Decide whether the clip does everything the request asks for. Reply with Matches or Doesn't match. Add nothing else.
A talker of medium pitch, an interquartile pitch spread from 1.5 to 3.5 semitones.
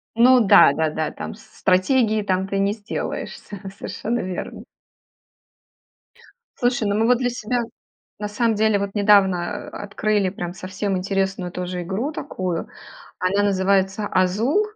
Doesn't match